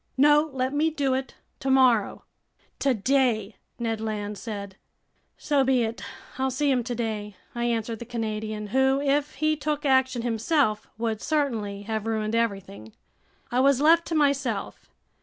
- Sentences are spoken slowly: No, average, 145 wpm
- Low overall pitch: No, high, 245 Hz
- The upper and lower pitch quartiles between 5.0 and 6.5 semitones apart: No, average, 4.1 semitones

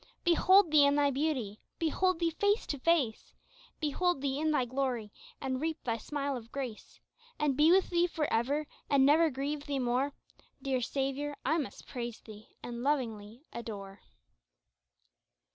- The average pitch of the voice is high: Yes, very high, 280 Hz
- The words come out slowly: No, average, 160 wpm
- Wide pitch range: No, average, 4.1 semitones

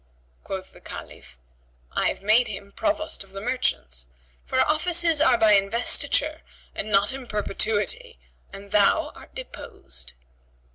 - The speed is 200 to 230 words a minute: No, slow, 135 wpm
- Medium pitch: No, high, 220 Hz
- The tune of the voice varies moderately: No, wide, 7.3 semitones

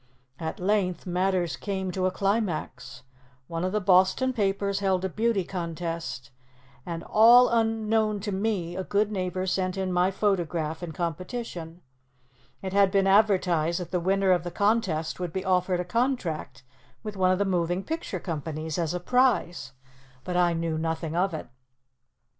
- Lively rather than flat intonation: No, average, 2.9 semitones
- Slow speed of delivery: No, average, 165 wpm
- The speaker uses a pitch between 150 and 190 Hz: Yes, medium, 185 Hz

